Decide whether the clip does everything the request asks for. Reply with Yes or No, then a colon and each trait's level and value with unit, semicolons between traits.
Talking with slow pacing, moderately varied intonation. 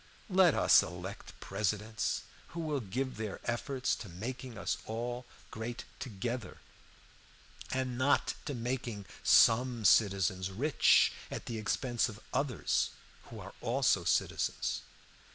Yes: slow, 120 wpm; average, 3.8 semitones